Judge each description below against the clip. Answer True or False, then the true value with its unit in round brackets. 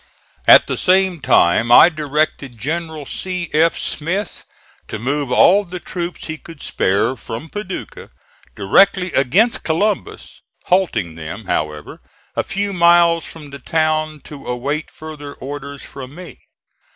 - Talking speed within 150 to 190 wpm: False (135 wpm)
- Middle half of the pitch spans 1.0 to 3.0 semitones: False (4.7 semitones)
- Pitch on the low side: False (155 Hz)